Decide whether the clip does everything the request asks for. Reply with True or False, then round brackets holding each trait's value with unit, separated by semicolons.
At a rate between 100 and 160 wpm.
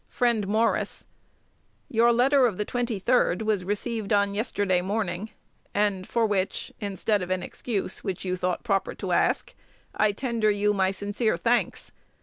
True (150 wpm)